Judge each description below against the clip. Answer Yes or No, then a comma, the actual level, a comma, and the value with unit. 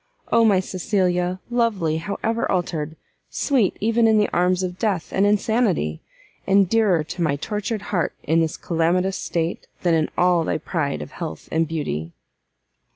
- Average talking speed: Yes, average, 160 wpm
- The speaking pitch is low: No, medium, 180 Hz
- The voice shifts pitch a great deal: No, average, 4.2 semitones